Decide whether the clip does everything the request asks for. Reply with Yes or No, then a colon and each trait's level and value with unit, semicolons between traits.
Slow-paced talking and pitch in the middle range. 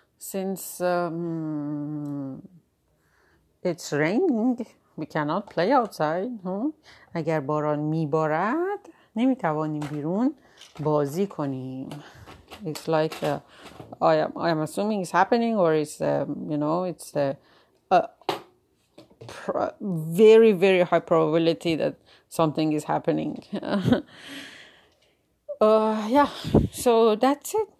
Yes: slow, 100 wpm; medium, 170 Hz